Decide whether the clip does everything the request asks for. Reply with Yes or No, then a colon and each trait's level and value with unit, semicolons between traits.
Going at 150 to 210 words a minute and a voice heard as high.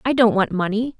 No: fast, 240 wpm; high, 225 Hz